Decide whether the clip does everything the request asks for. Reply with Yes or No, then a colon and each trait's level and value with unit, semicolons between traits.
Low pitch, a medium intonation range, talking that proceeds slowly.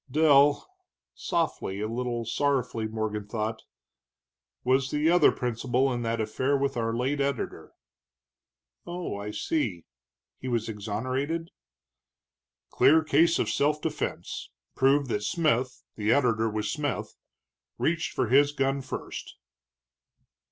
Yes: low, 130 Hz; average, 4.3 semitones; slow, 120 wpm